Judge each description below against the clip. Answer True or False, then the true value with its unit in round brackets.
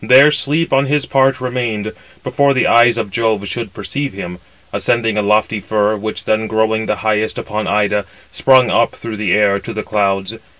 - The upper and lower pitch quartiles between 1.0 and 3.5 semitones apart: True (3.2 semitones)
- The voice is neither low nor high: False (110 Hz)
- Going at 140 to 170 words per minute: False (185 wpm)